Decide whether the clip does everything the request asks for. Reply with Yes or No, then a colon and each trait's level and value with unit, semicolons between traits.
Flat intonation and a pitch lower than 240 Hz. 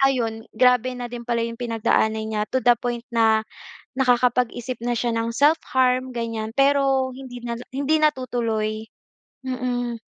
No: narrow, 2.0 semitones; high, 245 Hz